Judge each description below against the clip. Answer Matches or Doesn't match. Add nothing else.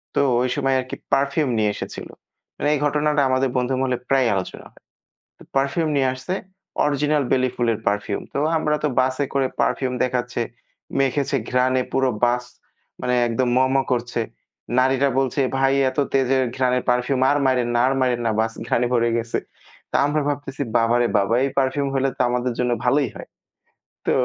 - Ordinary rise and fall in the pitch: Doesn't match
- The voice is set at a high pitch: Doesn't match